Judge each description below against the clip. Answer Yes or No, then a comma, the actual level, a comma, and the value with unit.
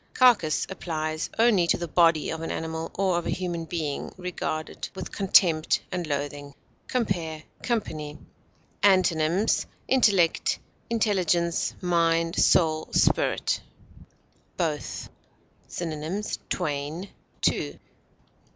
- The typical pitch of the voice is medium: Yes, medium, 170 Hz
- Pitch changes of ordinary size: Yes, average, 3.1 semitones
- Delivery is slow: Yes, slow, 100 wpm